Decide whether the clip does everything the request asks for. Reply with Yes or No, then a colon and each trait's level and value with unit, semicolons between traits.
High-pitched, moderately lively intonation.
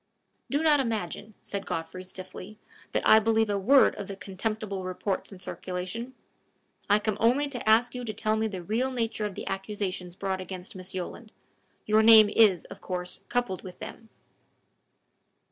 Yes: high, 210 Hz; average, 3.2 semitones